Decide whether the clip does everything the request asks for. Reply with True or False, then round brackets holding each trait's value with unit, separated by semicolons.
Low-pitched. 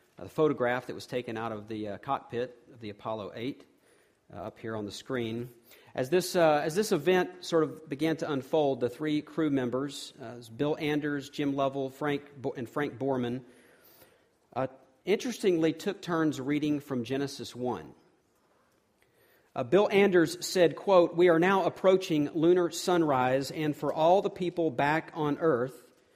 False (145 Hz)